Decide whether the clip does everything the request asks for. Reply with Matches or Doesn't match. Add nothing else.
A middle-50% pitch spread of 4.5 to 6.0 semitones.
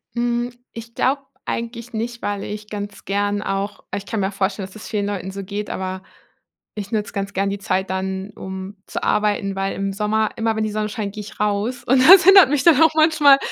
Doesn't match